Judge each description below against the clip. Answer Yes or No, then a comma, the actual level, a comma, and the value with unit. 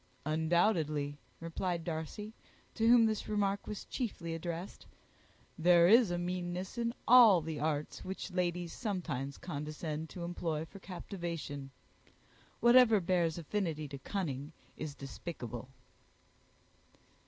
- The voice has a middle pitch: Yes, medium, 170 Hz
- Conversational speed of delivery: No, slow, 110 wpm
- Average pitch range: Yes, average, 4.1 semitones